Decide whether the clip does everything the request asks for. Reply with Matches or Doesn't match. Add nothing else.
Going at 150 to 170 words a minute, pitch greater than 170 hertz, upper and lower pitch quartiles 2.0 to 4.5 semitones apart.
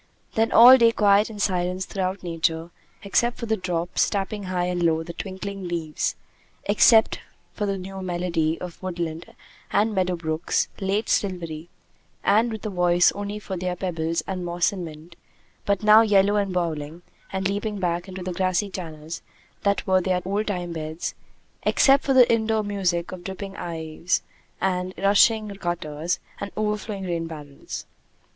Matches